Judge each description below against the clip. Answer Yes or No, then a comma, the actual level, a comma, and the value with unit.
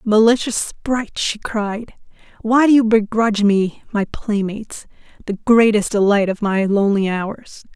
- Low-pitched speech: No, high, 215 Hz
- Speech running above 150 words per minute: No, average, 140 wpm